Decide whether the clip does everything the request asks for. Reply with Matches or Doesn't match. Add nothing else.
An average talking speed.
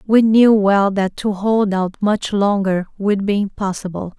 Matches